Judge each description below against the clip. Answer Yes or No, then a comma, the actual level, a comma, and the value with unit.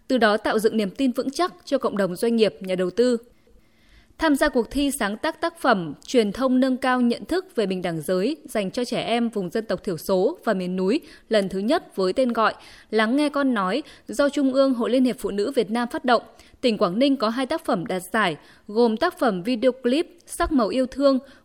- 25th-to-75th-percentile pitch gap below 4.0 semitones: No, average, 4.5 semitones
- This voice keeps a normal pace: Yes, average, 240 wpm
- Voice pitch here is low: No, high, 240 Hz